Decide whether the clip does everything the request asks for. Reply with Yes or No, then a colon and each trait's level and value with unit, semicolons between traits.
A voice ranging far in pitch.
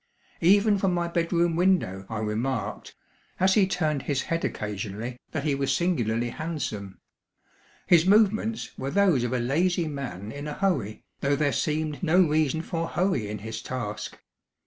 Yes: wide, 6.8 semitones